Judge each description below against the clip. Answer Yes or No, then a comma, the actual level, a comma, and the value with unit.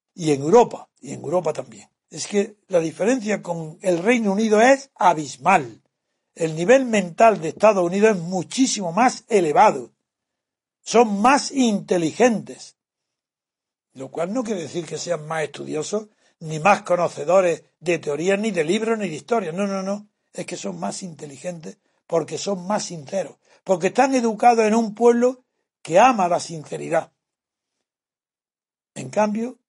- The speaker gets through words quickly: No, average, 150 wpm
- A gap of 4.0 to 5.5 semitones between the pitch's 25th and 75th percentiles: Yes, average, 5.0 semitones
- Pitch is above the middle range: Yes, high, 195 Hz